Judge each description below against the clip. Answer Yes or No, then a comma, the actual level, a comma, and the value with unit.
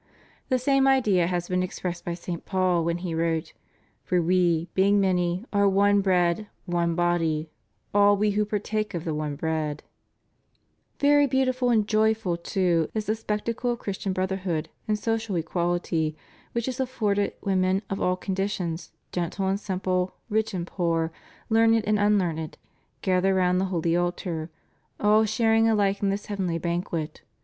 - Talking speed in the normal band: Yes, average, 160 wpm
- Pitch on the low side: No, high, 190 Hz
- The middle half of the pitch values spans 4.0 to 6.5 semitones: No, average, 3.5 semitones